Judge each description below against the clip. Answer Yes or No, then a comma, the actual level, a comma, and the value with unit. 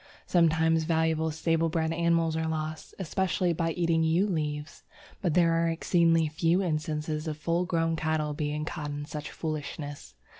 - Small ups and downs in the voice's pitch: Yes, narrow, 1.5 semitones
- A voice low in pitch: No, medium, 160 Hz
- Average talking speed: Yes, average, 155 wpm